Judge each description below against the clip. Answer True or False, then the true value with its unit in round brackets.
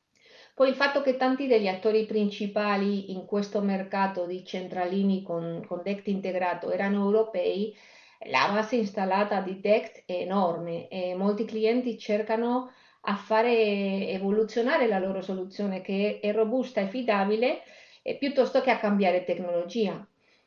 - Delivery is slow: False (140 wpm)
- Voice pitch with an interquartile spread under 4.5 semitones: True (2.7 semitones)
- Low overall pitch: False (205 Hz)